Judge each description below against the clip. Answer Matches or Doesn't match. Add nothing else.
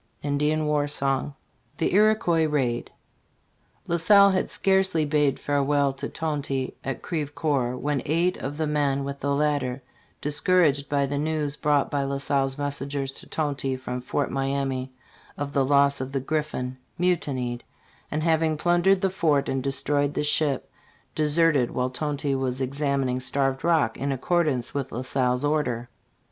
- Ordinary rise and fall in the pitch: Doesn't match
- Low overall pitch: Doesn't match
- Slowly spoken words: Doesn't match